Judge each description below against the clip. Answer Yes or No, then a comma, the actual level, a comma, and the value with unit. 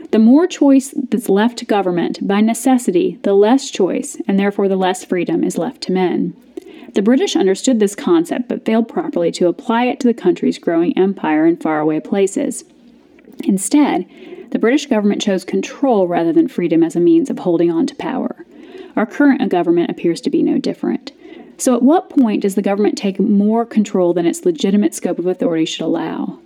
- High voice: Yes, high, 245 Hz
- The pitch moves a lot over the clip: Yes, wide, 7.6 semitones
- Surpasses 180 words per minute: Yes, average, 190 wpm